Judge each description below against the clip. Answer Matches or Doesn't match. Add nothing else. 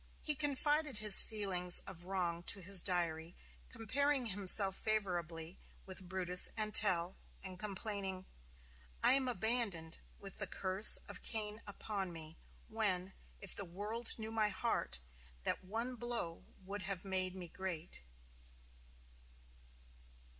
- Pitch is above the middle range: Matches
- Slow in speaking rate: Matches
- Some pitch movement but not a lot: Matches